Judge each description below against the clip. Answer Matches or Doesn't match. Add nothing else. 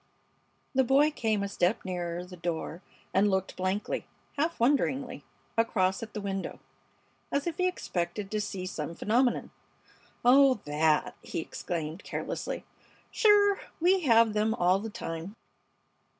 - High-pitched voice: Matches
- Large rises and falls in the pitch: Matches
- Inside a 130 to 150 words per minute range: Matches